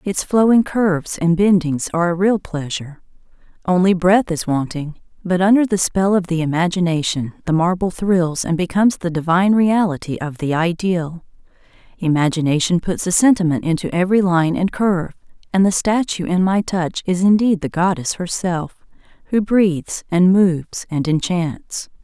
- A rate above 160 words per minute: No, average, 155 wpm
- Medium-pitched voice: Yes, medium, 180 Hz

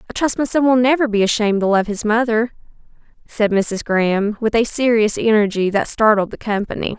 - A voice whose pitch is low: No, high, 220 Hz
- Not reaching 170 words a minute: No, average, 200 wpm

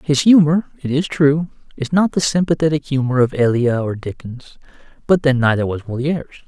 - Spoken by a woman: No, male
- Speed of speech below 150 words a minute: No, average, 175 wpm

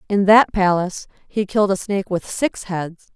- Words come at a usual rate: Yes, average, 190 wpm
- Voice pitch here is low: No, high, 195 Hz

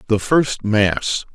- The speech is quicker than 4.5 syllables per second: No, 2.8 syllables/s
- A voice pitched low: Yes, low, 115 Hz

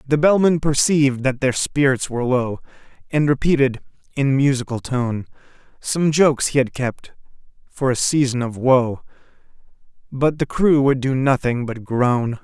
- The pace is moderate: Yes, average, 150 wpm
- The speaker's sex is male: Yes, male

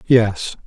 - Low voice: Yes, low, 115 Hz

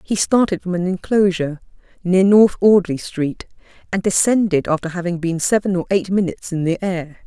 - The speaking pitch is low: No, medium, 185 Hz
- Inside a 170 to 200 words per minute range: Yes, average, 175 wpm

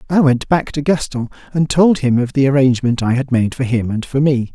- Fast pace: Yes, fast, 250 wpm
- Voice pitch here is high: No, low, 135 Hz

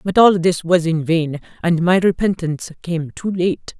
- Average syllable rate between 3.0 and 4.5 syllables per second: Yes, 4.4 syllables/s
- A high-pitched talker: No, medium, 170 Hz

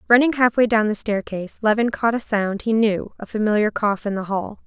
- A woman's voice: Yes, female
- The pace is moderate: No, fast, 220 wpm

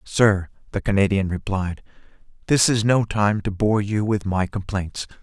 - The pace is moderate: Yes, average, 160 wpm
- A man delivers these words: Yes, male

